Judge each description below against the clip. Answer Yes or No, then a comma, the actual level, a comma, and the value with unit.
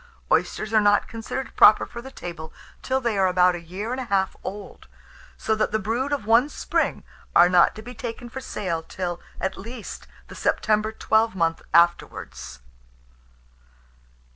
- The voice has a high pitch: Yes, high, 215 Hz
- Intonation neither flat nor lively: Yes, average, 4.2 semitones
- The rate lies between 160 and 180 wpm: Yes, average, 165 wpm